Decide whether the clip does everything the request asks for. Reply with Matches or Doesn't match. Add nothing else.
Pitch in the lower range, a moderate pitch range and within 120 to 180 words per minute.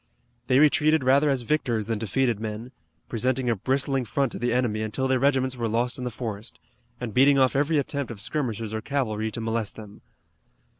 Doesn't match